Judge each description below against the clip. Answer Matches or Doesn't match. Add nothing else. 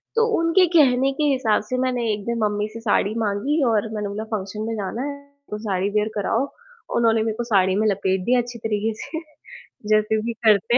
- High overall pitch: Matches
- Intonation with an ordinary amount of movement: Matches